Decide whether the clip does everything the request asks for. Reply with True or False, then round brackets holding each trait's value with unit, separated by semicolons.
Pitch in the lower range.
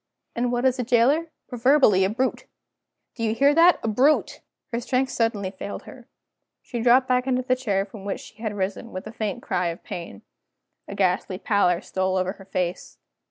False (225 Hz)